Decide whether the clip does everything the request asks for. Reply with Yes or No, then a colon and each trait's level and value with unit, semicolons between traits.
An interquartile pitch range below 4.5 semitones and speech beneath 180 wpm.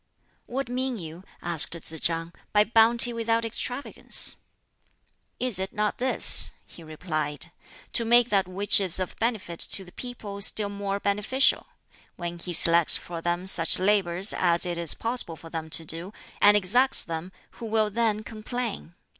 No: average, 5.0 semitones; average, 160 wpm